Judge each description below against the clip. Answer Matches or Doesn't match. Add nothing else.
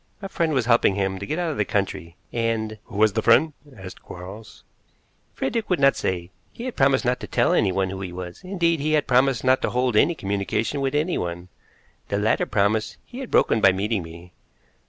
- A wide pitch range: Matches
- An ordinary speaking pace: Doesn't match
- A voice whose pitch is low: Matches